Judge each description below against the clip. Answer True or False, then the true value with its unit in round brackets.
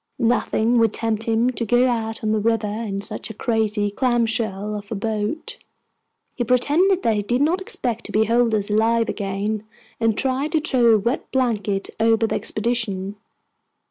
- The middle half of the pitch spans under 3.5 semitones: True (2.4 semitones)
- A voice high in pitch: True (225 Hz)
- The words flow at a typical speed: True (175 wpm)